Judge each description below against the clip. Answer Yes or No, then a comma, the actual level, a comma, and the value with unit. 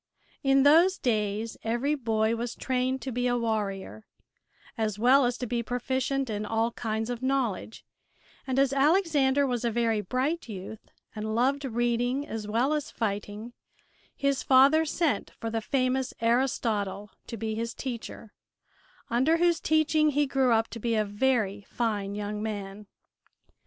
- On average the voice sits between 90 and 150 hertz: No, high, 240 Hz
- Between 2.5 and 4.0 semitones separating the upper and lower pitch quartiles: Yes, average, 3.6 semitones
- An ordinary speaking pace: Yes, average, 155 wpm